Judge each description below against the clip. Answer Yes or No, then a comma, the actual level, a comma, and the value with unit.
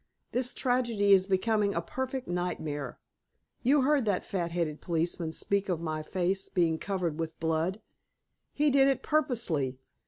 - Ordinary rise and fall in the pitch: No, wide, 6.9 semitones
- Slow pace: No, average, 150 wpm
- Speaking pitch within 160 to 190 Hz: Yes, medium, 185 Hz